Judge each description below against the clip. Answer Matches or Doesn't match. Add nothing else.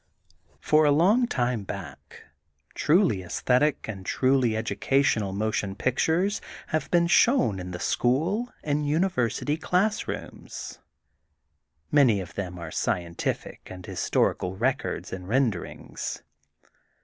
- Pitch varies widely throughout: Matches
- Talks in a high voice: Doesn't match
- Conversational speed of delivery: Doesn't match